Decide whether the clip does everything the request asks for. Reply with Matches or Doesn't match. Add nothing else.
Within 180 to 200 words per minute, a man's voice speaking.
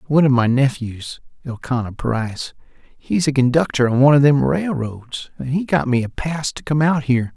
Matches